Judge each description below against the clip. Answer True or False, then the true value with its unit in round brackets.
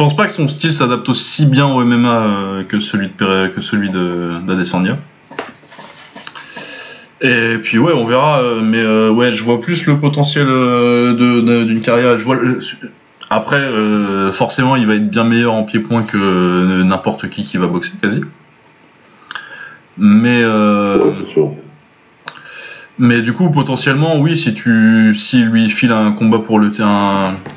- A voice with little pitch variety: False (3.2 semitones)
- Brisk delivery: False (160 wpm)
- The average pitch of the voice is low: True (115 Hz)